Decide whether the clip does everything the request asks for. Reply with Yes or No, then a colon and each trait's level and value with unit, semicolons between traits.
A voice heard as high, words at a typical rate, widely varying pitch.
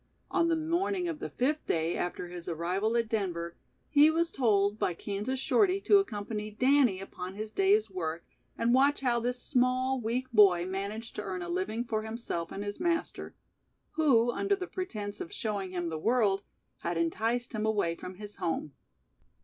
Yes: high, 220 Hz; average, 180 wpm; wide, 5.9 semitones